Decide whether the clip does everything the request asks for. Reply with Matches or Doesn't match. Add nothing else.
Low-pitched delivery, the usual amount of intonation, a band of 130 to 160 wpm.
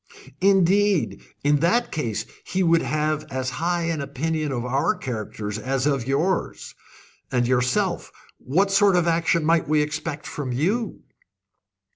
Doesn't match